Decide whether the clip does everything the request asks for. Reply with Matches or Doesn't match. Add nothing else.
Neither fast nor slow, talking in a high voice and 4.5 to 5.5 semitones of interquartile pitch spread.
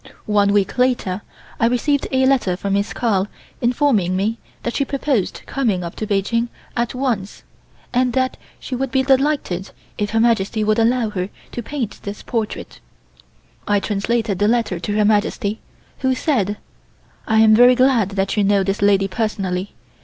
Doesn't match